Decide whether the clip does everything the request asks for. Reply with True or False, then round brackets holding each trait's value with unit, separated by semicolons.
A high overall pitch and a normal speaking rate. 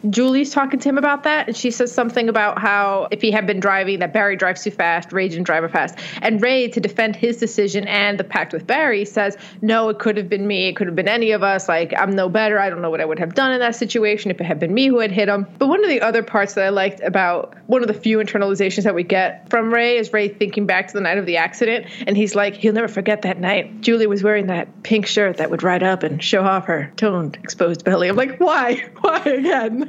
False (210 Hz; 275 wpm)